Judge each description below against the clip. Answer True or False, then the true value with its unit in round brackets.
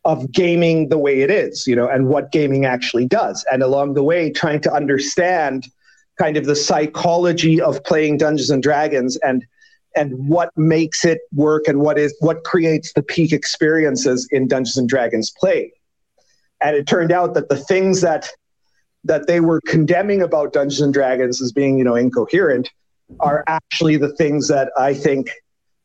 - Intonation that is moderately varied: True (3.1 semitones)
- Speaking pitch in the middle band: True (150 Hz)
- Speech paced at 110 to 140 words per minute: False (175 wpm)